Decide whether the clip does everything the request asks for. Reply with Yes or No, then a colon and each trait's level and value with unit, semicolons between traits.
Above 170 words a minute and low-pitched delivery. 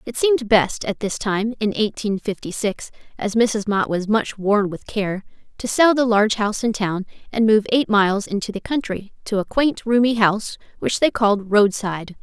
No: average, 200 wpm; high, 215 Hz